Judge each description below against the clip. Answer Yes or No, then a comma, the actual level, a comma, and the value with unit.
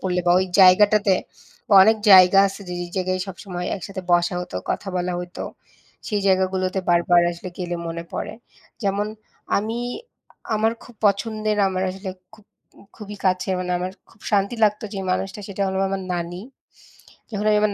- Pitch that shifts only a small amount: Yes, narrow, 2.3 semitones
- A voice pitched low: No, high, 190 Hz